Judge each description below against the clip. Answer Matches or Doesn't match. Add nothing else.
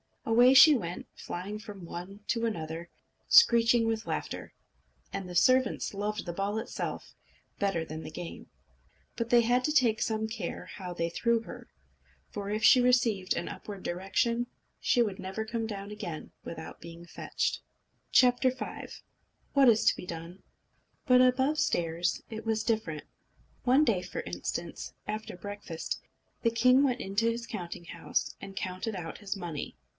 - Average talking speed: Matches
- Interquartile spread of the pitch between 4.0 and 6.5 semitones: Matches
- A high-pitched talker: Matches